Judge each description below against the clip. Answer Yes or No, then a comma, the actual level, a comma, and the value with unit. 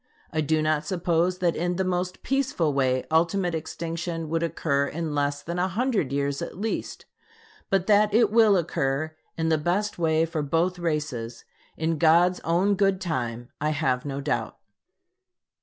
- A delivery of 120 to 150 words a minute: No, average, 165 wpm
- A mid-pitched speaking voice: Yes, medium, 165 Hz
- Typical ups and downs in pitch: Yes, average, 3.3 semitones